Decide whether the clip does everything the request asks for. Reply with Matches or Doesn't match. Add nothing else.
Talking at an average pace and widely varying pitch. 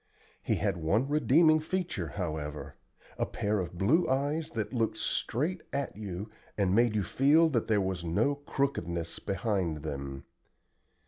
Matches